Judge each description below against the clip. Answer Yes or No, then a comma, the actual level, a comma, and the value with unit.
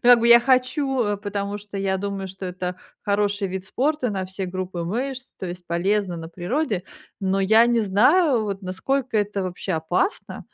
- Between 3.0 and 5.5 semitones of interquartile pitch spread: Yes, average, 4.1 semitones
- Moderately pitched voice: No, high, 200 Hz